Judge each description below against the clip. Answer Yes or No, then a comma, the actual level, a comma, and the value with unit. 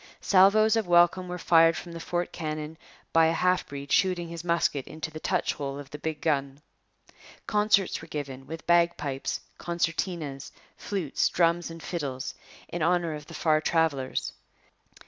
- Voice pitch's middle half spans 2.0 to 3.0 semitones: Yes, average, 2.7 semitones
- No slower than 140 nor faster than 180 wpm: Yes, average, 160 wpm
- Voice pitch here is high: No, medium, 165 Hz